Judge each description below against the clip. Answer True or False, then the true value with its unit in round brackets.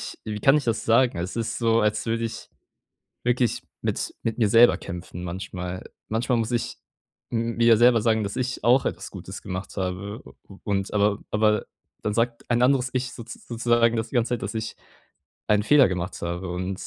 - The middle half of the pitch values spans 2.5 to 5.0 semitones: True (2.9 semitones)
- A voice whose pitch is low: True (115 Hz)